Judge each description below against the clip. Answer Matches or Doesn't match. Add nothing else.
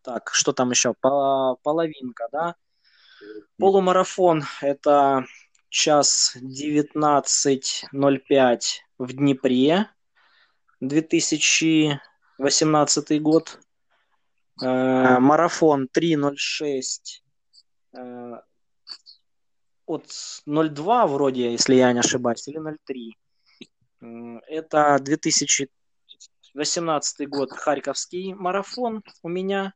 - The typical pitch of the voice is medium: Matches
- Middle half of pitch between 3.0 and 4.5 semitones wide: Matches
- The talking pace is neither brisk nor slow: Doesn't match